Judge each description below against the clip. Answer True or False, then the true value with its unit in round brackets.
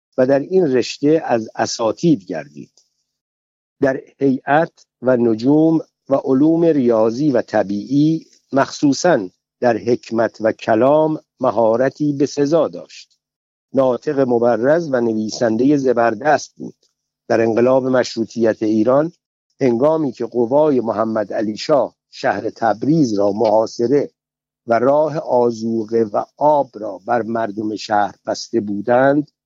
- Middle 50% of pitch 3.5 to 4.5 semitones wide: True (4.0 semitones)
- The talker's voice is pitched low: True (120 Hz)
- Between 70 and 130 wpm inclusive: True (115 wpm)